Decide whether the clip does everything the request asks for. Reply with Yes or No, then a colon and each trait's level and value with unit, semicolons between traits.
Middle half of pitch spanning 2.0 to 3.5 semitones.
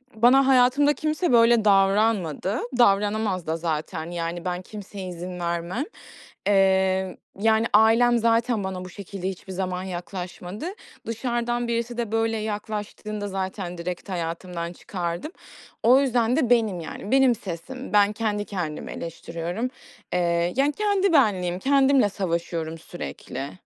No: average, 4.7 semitones